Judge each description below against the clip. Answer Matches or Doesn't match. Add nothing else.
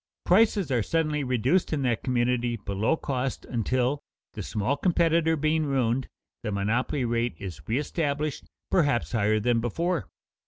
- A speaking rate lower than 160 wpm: Matches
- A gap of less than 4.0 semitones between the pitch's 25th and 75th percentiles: Doesn't match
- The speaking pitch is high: Doesn't match